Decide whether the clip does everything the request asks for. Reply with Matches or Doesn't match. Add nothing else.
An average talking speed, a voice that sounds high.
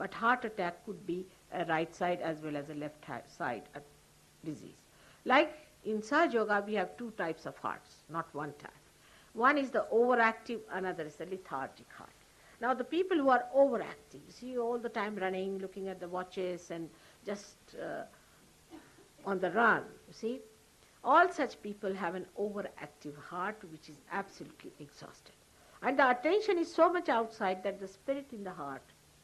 Matches